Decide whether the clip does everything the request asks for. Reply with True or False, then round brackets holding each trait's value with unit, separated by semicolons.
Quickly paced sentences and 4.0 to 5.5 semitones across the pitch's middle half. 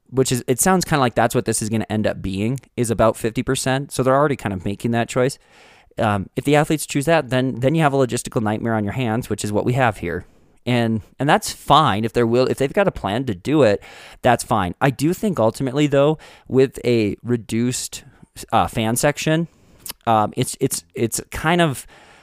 False (225 wpm; 3.5 semitones)